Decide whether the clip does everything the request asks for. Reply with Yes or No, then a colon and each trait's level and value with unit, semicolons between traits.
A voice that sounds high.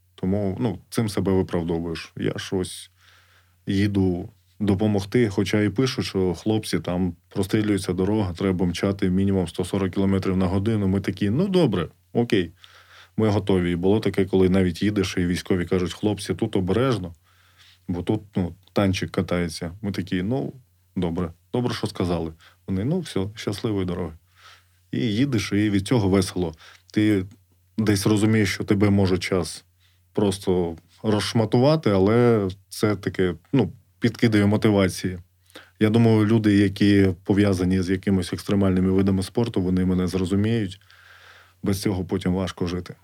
No: very low, 95 Hz